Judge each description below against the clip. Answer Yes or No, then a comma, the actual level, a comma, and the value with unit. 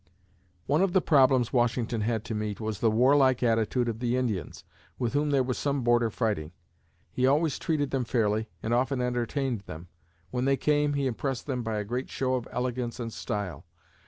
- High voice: No, low, 125 Hz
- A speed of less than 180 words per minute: No, average, 190 wpm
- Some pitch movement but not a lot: Yes, average, 3.0 semitones